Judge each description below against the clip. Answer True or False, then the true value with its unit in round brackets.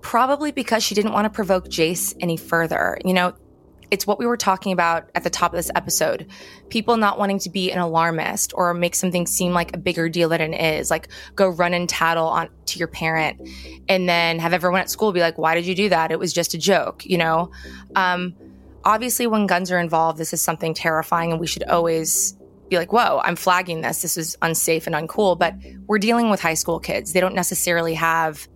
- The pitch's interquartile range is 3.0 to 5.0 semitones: False (2.4 semitones)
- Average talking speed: False (225 wpm)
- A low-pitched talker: False (175 Hz)